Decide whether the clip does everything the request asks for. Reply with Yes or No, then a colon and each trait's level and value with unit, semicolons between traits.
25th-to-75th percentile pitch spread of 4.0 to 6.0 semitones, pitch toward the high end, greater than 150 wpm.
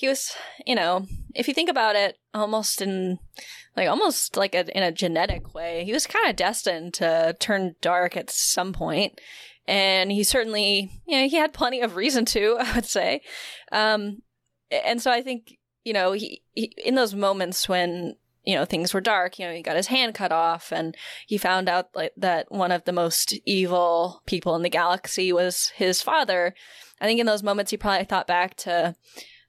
Yes: average, 4.3 semitones; high, 195 Hz; average, 200 wpm